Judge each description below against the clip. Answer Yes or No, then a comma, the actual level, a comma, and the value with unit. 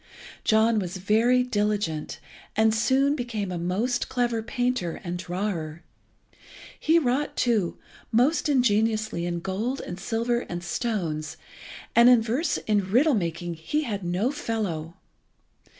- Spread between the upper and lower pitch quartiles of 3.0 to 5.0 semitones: No, wide, 5.6 semitones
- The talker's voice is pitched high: Yes, high, 215 Hz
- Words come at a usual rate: No, slow, 130 wpm